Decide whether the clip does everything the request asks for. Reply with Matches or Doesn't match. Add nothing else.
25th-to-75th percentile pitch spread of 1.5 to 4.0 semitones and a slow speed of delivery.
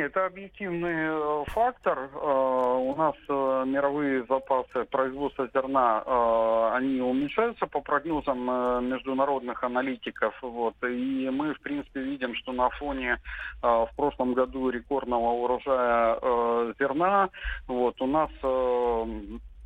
Matches